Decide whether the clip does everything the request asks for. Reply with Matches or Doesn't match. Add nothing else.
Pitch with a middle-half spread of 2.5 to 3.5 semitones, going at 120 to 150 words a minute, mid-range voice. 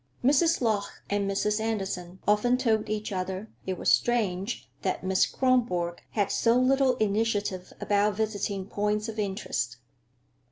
Doesn't match